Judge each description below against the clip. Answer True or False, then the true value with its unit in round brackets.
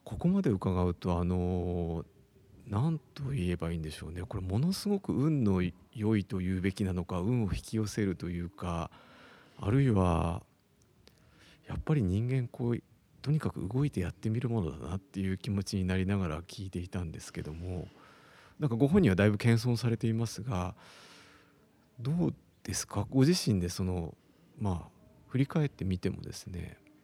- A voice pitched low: True (100 Hz)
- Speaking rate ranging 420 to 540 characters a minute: False (320 characters per minute)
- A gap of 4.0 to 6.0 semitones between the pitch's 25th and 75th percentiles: True (5.1 semitones)